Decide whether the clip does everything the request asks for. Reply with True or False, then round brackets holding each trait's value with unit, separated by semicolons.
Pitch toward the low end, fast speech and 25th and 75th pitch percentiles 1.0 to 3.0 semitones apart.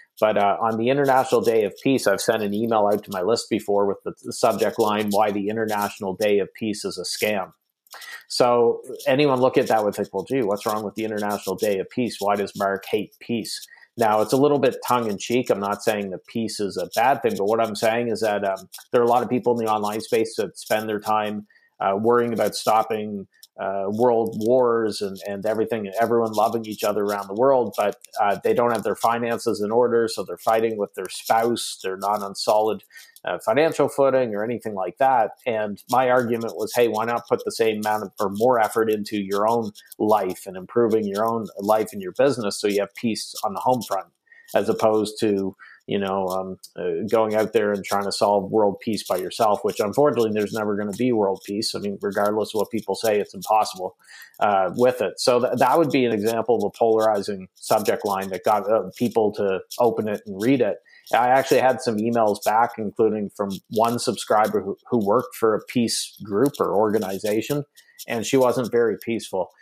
True (110 Hz; 215 wpm; 2.5 semitones)